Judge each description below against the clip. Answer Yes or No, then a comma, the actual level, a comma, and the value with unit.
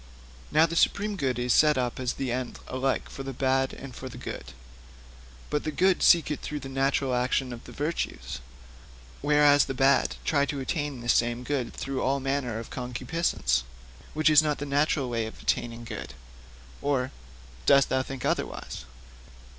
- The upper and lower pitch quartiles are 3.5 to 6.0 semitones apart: No, average, 2.7 semitones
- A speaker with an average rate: Yes, average, 180 wpm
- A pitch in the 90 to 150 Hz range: Yes, low, 135 Hz